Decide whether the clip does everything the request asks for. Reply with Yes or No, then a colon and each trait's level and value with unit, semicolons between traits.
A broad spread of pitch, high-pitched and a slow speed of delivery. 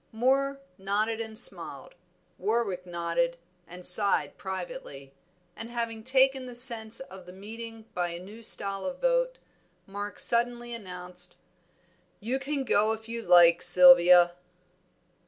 No: average, 4.9 semitones; high, 220 Hz; slow, 130 wpm